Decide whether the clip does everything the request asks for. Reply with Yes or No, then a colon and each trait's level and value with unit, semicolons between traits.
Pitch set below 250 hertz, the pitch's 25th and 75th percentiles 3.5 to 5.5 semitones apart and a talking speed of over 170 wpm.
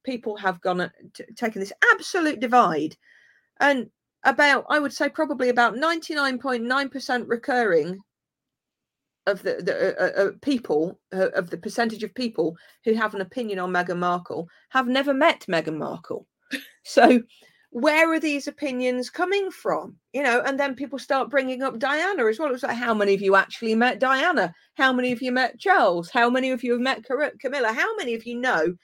No: very high, 255 Hz; average, 4.7 semitones; average, 185 wpm